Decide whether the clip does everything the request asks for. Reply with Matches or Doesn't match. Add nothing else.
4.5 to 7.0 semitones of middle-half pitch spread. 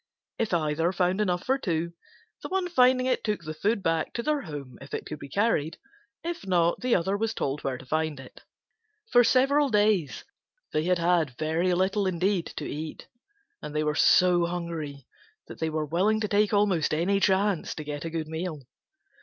Matches